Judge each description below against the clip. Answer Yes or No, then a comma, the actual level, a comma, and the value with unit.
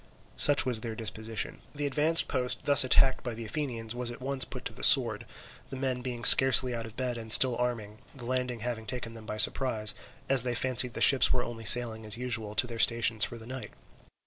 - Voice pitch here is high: No, low, 120 Hz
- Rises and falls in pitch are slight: Yes, narrow, 2.3 semitones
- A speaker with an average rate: No, fast, 220 wpm